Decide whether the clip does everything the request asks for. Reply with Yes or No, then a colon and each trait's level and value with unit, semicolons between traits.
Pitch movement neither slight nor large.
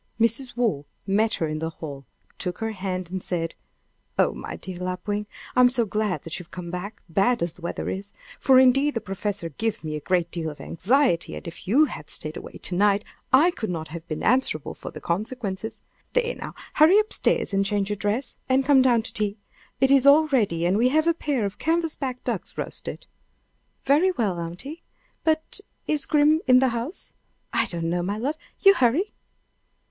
No: wide, 6.9 semitones